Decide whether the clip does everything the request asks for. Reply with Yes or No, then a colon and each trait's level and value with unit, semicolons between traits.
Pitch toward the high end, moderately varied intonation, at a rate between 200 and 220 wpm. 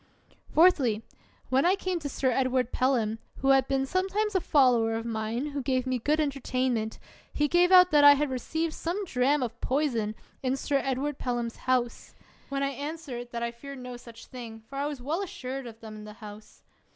Yes: very high, 260 Hz; average, 3.7 semitones; fast, 205 wpm